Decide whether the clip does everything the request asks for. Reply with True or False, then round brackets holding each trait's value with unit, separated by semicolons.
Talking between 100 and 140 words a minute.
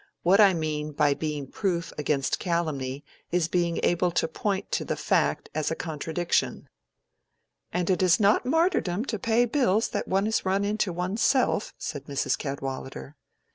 False (165 wpm)